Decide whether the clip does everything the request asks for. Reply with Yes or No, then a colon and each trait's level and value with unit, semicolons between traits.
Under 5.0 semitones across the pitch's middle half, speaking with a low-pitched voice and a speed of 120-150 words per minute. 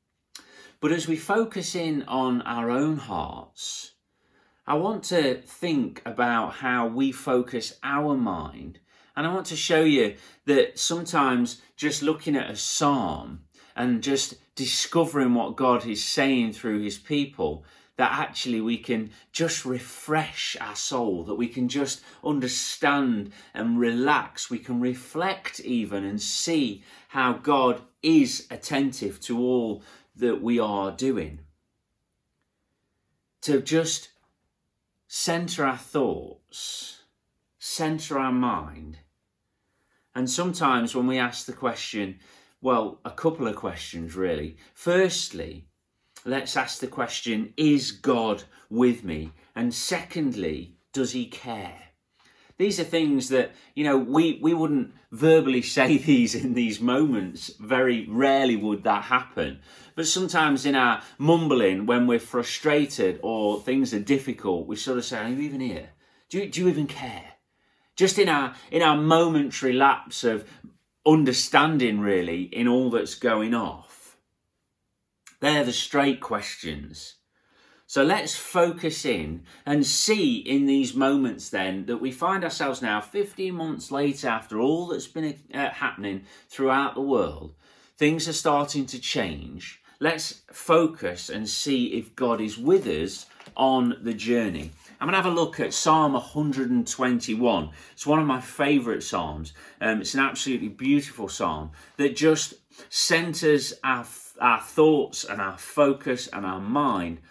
No: average, 5.3 semitones; low, 130 Hz; average, 140 wpm